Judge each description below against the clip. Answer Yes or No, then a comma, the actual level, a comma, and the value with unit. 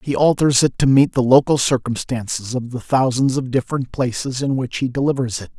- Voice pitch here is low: Yes, low, 130 Hz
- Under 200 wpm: No, fast, 205 wpm